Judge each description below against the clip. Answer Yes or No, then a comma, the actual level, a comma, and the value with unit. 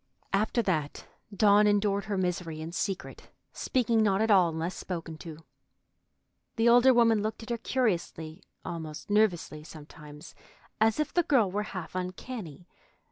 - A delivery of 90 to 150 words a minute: Yes, average, 145 wpm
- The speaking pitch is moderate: No, high, 195 Hz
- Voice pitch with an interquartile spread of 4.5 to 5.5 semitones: Yes, average, 5.0 semitones